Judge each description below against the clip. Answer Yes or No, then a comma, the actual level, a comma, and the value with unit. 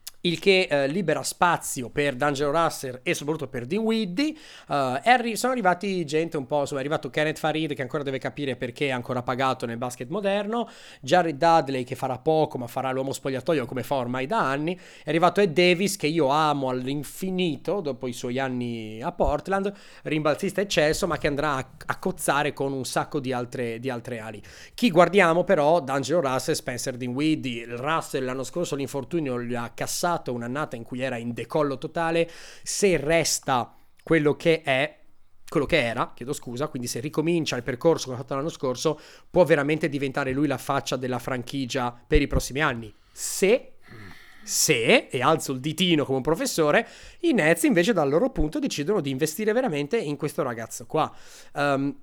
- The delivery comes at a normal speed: No, fast, 180 wpm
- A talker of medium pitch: Yes, medium, 145 Hz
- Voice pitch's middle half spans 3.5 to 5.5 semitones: Yes, average, 4.2 semitones